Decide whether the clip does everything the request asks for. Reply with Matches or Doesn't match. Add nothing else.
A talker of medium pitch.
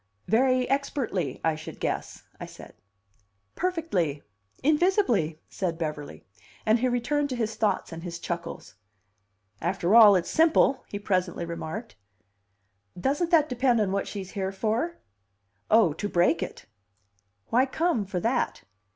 Doesn't match